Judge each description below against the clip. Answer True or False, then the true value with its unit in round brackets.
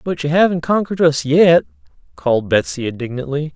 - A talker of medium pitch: True (145 Hz)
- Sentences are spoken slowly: False (150 wpm)